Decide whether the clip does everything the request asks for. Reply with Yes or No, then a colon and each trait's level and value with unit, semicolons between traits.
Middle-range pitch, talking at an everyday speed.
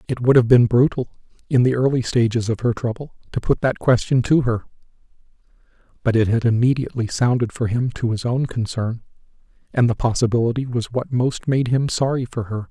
No: low, 120 Hz; average, 190 wpm